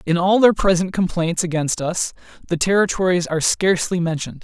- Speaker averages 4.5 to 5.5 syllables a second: No, 5.8 syllables/s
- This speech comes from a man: Yes, male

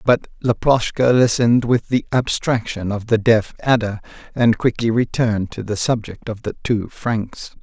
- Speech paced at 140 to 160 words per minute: Yes, average, 155 wpm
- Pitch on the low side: Yes, low, 115 Hz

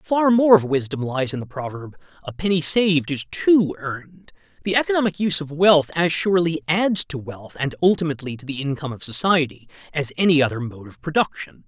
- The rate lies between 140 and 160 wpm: No, average, 190 wpm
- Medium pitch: Yes, medium, 160 Hz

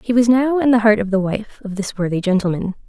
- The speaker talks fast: Yes, fast, 270 wpm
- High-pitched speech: Yes, high, 215 Hz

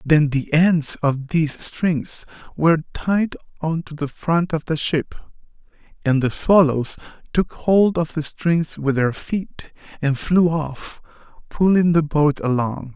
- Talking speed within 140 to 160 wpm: Yes, average, 155 wpm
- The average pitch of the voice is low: No, medium, 155 Hz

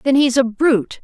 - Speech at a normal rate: No, fast, 235 wpm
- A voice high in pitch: Yes, very high, 260 Hz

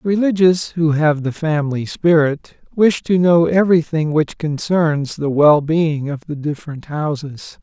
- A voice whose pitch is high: No, medium, 155 Hz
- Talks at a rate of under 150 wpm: Yes, average, 140 wpm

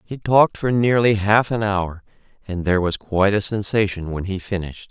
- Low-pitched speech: Yes, low, 100 Hz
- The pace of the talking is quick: No, average, 195 wpm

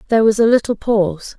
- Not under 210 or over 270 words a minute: Yes, fast, 215 wpm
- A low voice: No, high, 215 Hz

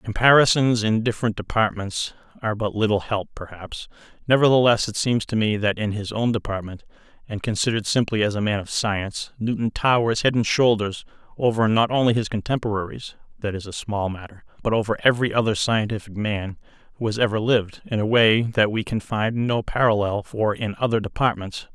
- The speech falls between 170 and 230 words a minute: Yes, average, 175 wpm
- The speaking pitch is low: Yes, low, 110 Hz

